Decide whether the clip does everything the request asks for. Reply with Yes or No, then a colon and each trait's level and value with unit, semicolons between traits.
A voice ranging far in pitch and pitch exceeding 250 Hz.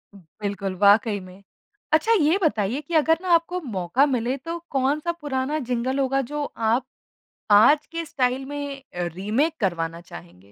Yes: wide, 6.7 semitones; very high, 260 Hz